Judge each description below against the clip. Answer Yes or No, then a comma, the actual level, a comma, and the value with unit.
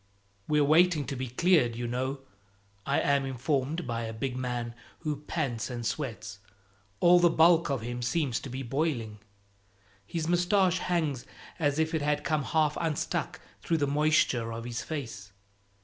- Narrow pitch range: No, average, 4.6 semitones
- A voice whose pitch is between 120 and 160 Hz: Yes, medium, 140 Hz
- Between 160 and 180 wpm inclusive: Yes, average, 165 wpm